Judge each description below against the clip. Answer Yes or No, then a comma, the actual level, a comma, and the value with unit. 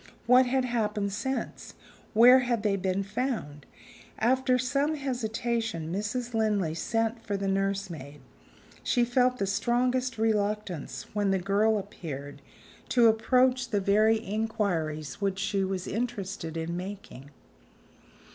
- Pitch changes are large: No, average, 3.9 semitones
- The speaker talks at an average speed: No, slow, 125 wpm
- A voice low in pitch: No, high, 215 Hz